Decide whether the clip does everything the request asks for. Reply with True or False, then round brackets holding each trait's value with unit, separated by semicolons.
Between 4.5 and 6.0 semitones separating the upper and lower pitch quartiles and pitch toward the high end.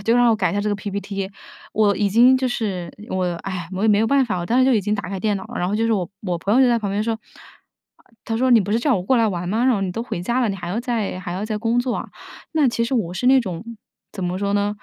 False (3.5 semitones; 210 Hz)